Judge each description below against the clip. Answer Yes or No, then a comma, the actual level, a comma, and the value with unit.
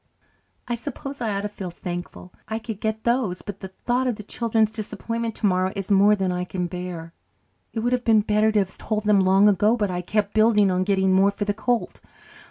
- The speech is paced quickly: Yes, fast, 220 wpm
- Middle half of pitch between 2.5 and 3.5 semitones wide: Yes, average, 2.8 semitones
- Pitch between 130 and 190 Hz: No, high, 210 Hz